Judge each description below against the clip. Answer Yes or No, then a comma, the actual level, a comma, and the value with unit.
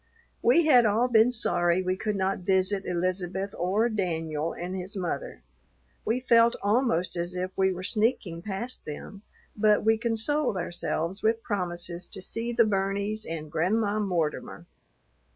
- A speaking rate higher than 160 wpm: No, average, 150 wpm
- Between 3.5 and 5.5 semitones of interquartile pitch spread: Yes, average, 3.8 semitones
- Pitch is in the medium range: No, high, 195 Hz